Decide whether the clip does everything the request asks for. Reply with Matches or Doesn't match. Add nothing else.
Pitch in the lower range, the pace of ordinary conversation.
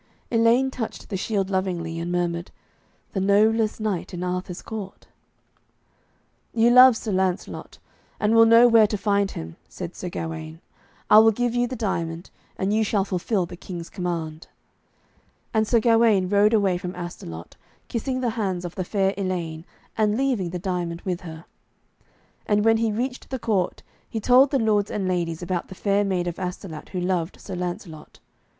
Doesn't match